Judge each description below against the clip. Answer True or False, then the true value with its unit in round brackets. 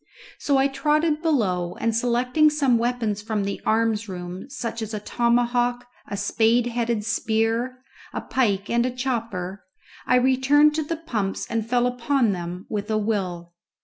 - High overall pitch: True (235 Hz)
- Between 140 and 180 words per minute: True (160 wpm)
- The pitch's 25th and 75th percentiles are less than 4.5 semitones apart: True (3.4 semitones)